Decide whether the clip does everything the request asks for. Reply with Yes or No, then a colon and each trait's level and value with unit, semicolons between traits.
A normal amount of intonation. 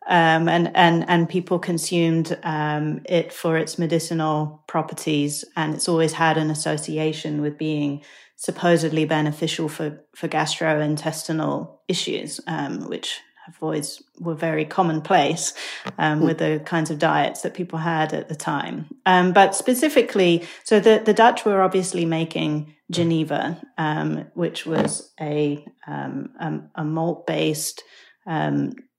No: narrow, 2.0 semitones